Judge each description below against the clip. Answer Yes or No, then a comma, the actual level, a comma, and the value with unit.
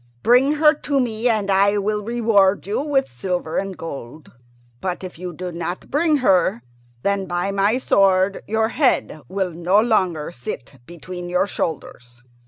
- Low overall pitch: No, high, 195 Hz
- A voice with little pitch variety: No, average, 4.1 semitones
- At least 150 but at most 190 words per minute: Yes, average, 160 wpm